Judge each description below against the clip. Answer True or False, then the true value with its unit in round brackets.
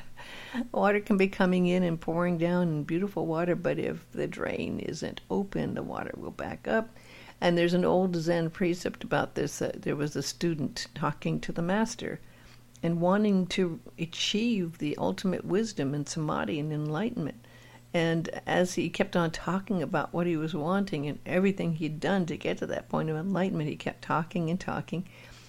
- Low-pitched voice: False (170 Hz)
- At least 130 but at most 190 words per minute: True (185 wpm)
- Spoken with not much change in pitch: False (3.3 semitones)